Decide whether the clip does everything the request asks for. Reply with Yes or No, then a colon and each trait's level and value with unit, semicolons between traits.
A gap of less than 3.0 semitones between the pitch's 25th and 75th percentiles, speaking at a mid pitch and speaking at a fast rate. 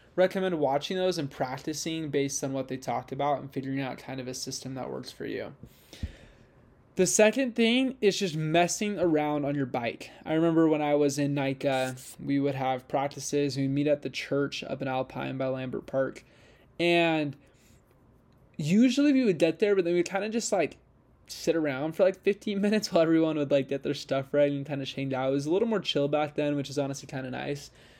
No: average, 4.1 semitones; medium, 145 Hz; fast, 215 wpm